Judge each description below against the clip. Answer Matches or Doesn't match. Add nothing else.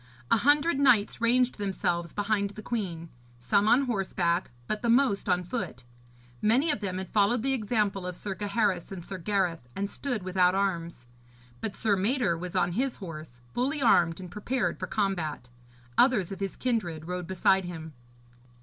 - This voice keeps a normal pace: Matches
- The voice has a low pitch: Doesn't match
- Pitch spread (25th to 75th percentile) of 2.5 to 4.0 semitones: Doesn't match